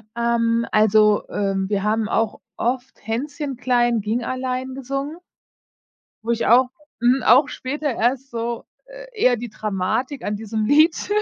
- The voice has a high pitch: Yes, high, 240 Hz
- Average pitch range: Yes, average, 3.2 semitones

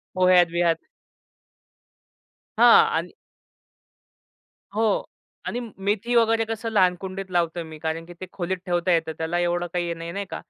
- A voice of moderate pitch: Yes, medium, 180 Hz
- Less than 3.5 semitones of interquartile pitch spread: Yes, average, 2.9 semitones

